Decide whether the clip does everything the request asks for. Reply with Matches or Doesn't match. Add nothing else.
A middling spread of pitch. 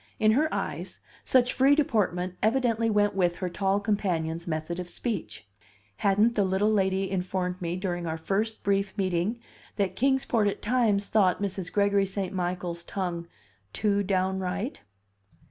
Matches